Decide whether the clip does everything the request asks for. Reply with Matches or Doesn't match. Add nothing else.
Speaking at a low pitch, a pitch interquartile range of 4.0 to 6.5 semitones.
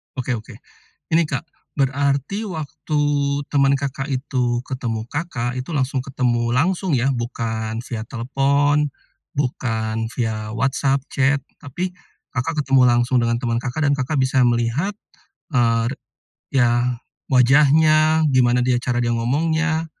Doesn't match